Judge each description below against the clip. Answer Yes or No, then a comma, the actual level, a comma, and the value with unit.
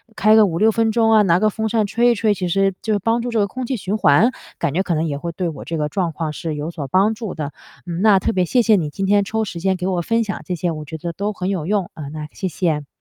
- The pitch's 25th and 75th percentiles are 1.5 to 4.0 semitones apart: No, average, 4.5 semitones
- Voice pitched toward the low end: No, high, 190 Hz